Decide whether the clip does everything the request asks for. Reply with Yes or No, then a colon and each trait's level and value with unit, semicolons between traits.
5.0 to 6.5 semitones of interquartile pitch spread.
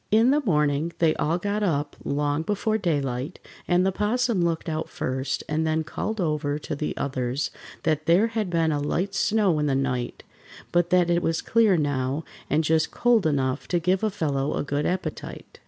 No: average, 4.5 semitones